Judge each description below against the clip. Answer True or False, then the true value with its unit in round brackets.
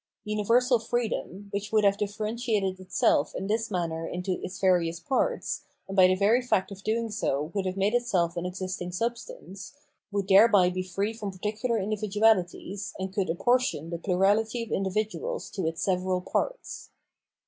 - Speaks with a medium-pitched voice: False (200 Hz)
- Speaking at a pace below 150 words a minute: False (165 wpm)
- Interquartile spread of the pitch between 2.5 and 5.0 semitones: True (3.2 semitones)